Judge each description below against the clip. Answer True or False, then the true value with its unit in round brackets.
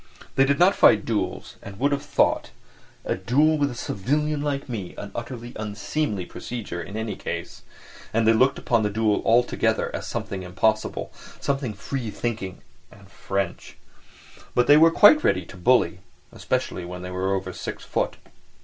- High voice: False (115 Hz)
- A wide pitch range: True (5.9 semitones)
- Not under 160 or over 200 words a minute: True (165 wpm)